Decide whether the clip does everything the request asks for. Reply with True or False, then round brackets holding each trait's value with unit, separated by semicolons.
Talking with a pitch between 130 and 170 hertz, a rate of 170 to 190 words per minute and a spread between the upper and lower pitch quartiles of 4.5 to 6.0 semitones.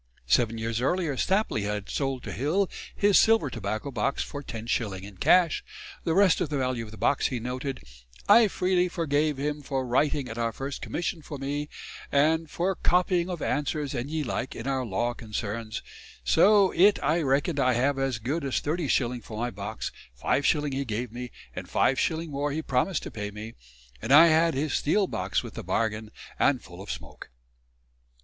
True (135 Hz; 185 wpm; 5.5 semitones)